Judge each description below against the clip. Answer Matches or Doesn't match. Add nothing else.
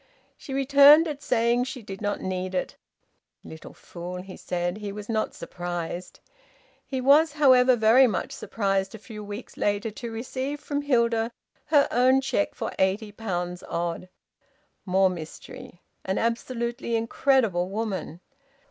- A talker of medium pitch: Doesn't match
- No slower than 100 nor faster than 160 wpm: Matches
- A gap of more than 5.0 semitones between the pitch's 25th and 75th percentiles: Matches